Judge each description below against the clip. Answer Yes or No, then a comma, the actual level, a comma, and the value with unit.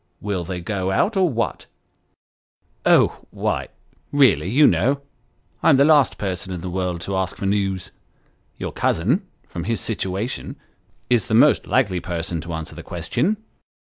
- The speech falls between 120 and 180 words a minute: Yes, average, 165 wpm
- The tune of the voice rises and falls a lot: Yes, wide, 6.4 semitones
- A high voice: No, low, 100 Hz